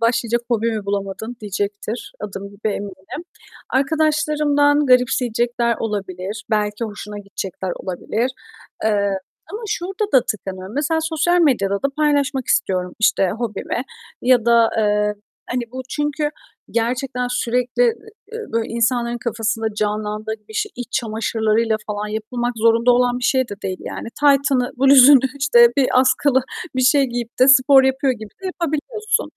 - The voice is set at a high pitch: Yes, high, 240 Hz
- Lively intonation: No, average, 4.3 semitones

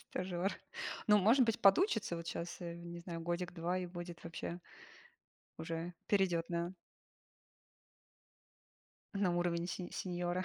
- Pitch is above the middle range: No, medium, 175 Hz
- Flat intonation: Yes, narrow, 1.6 semitones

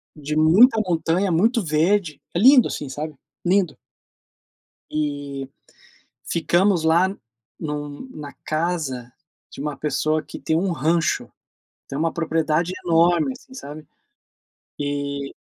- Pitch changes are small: No, average, 3.2 semitones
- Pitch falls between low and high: Yes, medium, 160 Hz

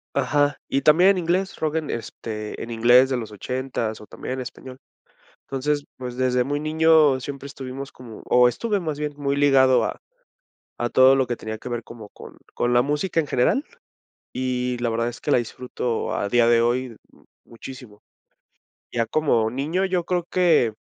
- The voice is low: Yes, low, 130 Hz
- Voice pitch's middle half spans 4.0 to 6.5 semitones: No, average, 3.6 semitones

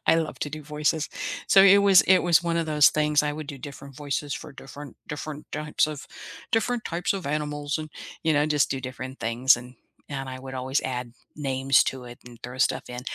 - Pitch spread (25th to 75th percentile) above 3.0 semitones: No, average, 2.7 semitones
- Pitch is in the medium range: Yes, medium, 145 Hz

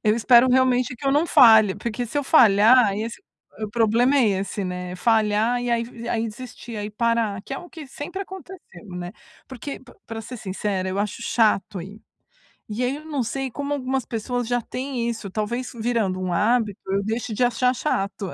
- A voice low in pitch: No, high, 230 Hz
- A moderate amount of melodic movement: Yes, average, 3.4 semitones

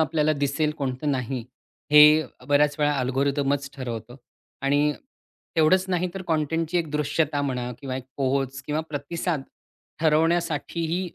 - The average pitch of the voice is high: No, medium, 150 Hz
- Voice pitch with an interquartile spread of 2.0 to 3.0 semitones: Yes, narrow, 2.6 semitones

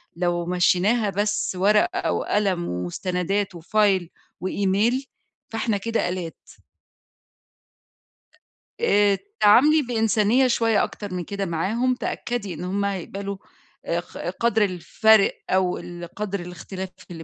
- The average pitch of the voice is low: No, high, 200 Hz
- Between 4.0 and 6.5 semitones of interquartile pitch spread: No, average, 3.3 semitones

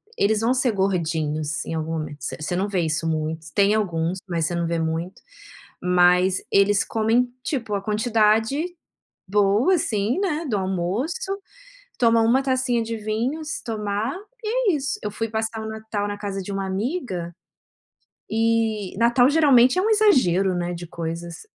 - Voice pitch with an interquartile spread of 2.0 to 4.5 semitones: No, average, 5.3 semitones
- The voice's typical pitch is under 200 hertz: No, high, 210 Hz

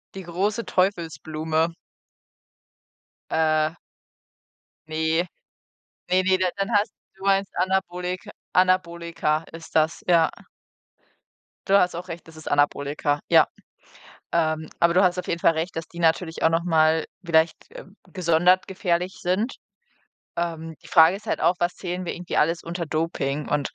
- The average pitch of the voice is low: No, medium, 170 Hz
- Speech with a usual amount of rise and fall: No, narrow, 2.3 semitones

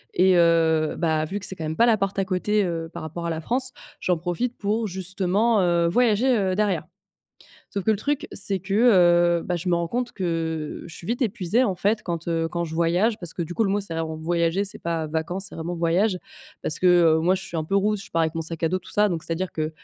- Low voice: No, medium, 180 Hz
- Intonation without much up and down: No, average, 3.5 semitones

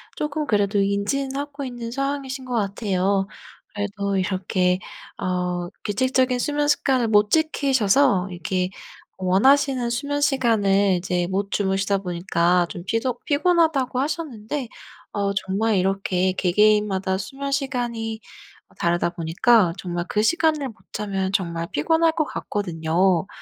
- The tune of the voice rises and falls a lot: Yes, wide, 5.9 semitones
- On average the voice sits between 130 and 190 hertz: No, high, 205 Hz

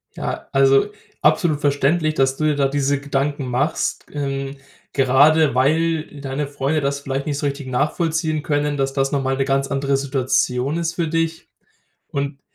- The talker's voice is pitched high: No, medium, 140 Hz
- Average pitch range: No, narrow, 2.1 semitones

